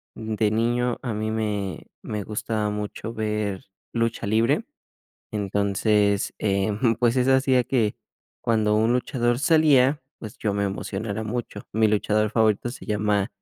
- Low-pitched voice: Yes, low, 110 Hz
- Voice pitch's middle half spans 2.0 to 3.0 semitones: Yes, narrow, 2.4 semitones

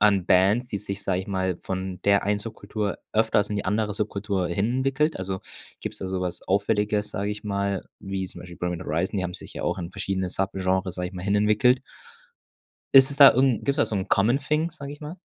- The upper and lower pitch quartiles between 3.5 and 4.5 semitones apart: No, narrow, 2.6 semitones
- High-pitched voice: No, low, 100 Hz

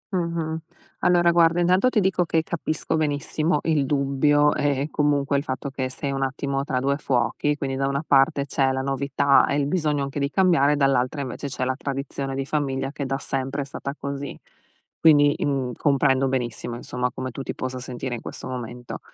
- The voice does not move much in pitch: Yes, narrow, 1.8 semitones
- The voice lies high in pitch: No, medium, 140 Hz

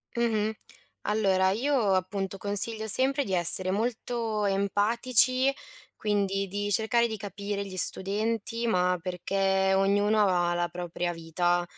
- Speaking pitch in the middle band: No, high, 200 Hz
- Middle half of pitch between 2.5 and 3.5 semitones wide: Yes, average, 2.8 semitones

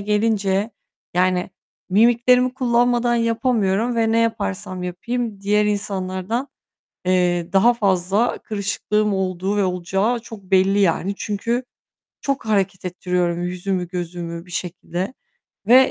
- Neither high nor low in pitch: No, high, 200 Hz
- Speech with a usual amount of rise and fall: Yes, average, 3.9 semitones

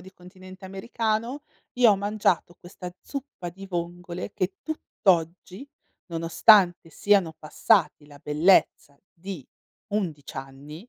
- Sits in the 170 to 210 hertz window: Yes, medium, 185 Hz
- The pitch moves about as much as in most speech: Yes, average, 3.6 semitones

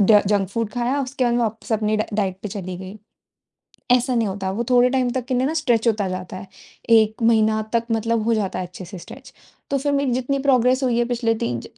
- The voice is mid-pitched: No, high, 230 Hz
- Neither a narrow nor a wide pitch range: Yes, average, 3.4 semitones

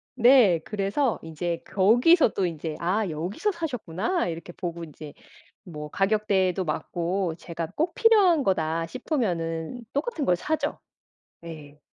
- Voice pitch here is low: No, medium, 185 Hz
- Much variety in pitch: Yes, wide, 7.3 semitones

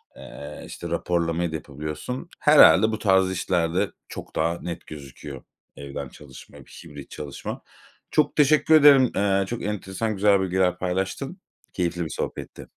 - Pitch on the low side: Yes, very low, 90 Hz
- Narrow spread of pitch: No, average, 4.9 semitones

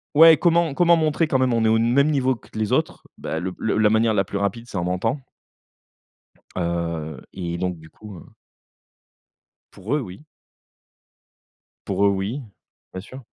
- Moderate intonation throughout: No, wide, 6.8 semitones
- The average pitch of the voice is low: Yes, low, 110 Hz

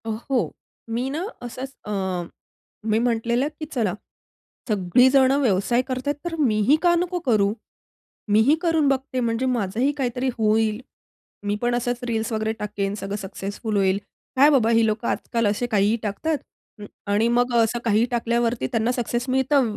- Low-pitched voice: No, high, 235 Hz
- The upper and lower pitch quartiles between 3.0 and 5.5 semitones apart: Yes, average, 3.3 semitones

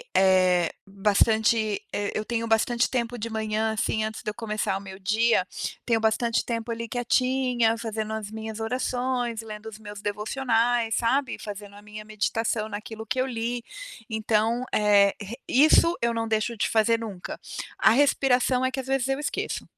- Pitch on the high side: Yes, high, 225 Hz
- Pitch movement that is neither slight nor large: No, narrow, 2.1 semitones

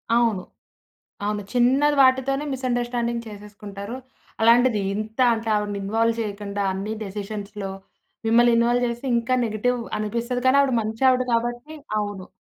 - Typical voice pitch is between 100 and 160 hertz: No, high, 230 Hz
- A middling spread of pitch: Yes, average, 3.0 semitones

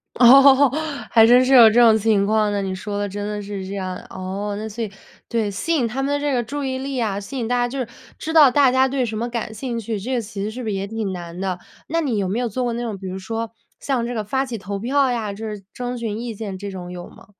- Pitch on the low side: No, high, 225 Hz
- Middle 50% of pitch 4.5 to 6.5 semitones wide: No, average, 3.7 semitones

